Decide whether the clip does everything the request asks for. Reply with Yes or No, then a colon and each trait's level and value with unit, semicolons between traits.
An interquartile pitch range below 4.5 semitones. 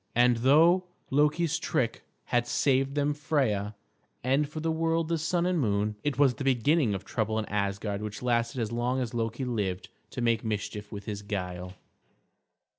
No: wide, 5.6 semitones